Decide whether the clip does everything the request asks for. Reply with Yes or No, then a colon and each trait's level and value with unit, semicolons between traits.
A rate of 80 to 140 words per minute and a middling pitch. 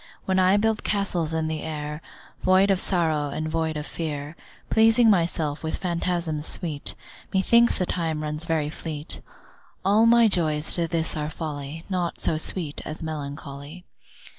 No: average, 155 wpm; medium, 160 Hz